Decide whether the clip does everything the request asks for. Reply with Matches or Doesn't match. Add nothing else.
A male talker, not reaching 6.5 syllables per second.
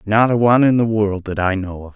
Matches